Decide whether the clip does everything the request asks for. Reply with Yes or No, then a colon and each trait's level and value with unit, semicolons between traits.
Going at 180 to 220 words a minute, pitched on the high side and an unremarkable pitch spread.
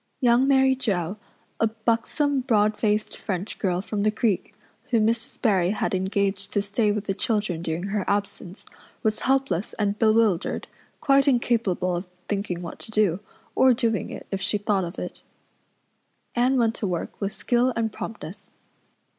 No: average, 165 wpm; high, 210 Hz; average, 3.0 semitones